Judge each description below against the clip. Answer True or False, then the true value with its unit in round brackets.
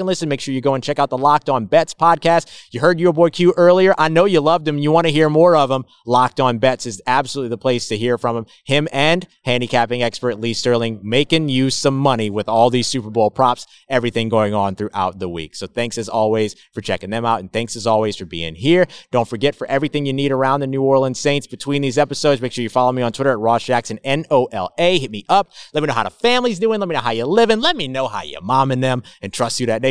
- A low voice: True (130 Hz)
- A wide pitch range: False (4.3 semitones)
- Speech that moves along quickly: True (275 wpm)